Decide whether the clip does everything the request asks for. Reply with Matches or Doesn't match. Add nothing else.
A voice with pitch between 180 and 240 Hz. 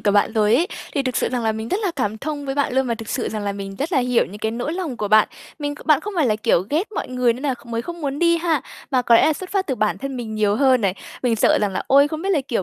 Doesn't match